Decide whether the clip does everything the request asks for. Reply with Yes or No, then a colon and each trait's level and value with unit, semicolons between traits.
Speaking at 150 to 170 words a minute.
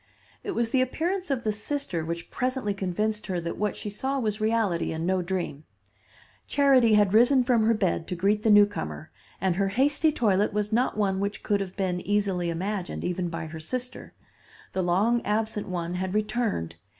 No: average, 185 wpm